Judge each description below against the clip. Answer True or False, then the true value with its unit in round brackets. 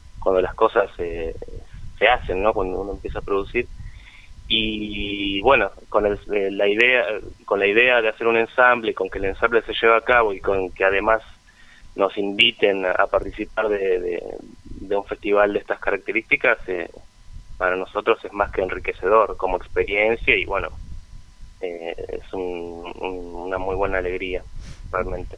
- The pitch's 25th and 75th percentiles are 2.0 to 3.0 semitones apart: False (3.6 semitones)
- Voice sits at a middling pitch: False (100 Hz)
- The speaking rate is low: False (165 wpm)